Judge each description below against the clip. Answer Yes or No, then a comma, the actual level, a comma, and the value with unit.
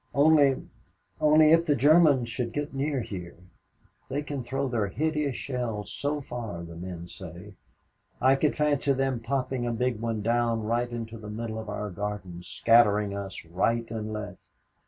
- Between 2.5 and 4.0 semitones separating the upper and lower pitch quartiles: No, average, 4.8 semitones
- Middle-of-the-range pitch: No, low, 115 Hz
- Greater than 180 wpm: No, average, 165 wpm